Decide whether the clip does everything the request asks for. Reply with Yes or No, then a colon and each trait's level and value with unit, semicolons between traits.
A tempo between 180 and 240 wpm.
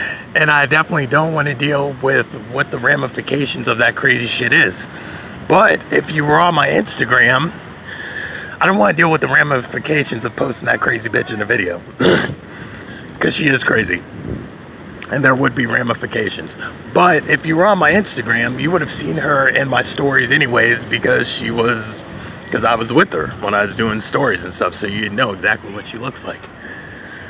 Yes: average, 200 wpm